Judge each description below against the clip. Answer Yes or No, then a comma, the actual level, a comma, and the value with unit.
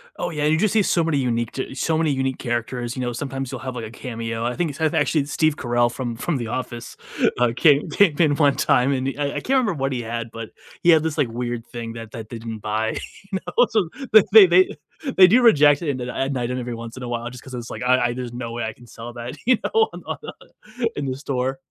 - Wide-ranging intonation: No, average, 4.2 semitones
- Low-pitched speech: Yes, low, 130 Hz